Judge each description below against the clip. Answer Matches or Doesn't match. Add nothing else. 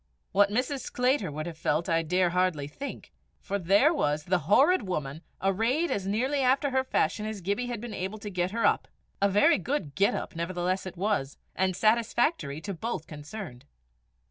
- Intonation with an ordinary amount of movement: Doesn't match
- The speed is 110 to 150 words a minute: Doesn't match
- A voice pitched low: Doesn't match